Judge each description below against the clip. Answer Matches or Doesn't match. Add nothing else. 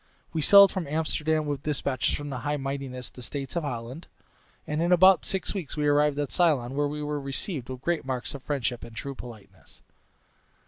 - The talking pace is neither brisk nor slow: Matches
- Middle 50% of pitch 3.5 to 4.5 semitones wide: Doesn't match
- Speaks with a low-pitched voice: Doesn't match